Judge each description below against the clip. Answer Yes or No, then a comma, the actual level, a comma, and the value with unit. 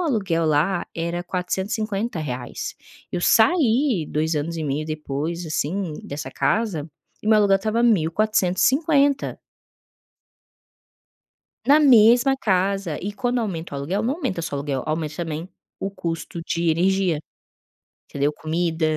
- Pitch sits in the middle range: Yes, medium, 180 Hz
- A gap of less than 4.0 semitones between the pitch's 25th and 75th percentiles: No, wide, 5.5 semitones